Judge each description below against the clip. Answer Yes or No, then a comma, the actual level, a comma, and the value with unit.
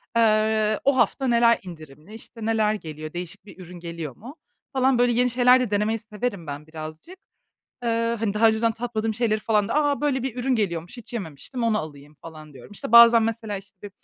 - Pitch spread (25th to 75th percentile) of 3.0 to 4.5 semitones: No, average, 5.2 semitones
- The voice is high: Yes, high, 215 Hz